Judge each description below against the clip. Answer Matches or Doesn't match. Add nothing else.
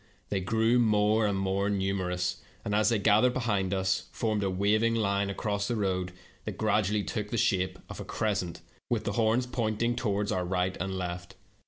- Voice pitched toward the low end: Matches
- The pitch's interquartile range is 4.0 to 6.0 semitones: Doesn't match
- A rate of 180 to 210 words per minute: Matches